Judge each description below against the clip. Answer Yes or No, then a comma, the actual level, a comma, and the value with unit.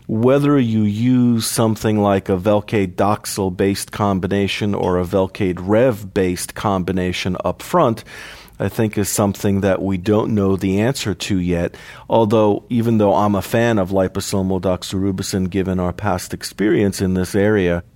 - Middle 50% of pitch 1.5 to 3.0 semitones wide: Yes, narrow, 2.4 semitones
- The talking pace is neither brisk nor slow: Yes, average, 155 wpm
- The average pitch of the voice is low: Yes, low, 100 Hz